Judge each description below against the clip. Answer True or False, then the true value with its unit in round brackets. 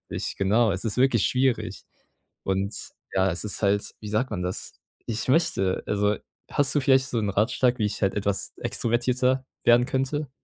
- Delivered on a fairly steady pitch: False (4.5 semitones)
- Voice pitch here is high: False (115 Hz)